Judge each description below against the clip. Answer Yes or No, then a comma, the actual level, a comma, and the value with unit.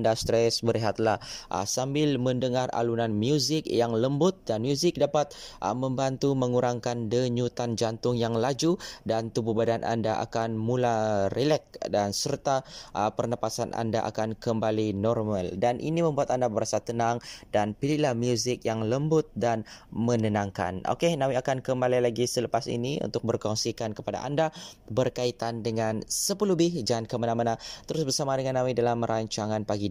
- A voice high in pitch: No, low, 120 Hz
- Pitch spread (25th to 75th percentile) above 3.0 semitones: No, average, 2.7 semitones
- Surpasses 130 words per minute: Yes, average, 140 wpm